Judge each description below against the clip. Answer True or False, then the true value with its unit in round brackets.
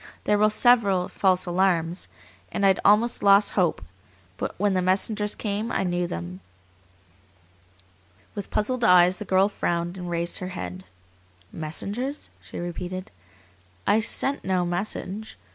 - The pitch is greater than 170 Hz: True (190 Hz)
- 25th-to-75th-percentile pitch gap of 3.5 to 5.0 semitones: False (2.9 semitones)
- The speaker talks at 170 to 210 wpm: False (135 wpm)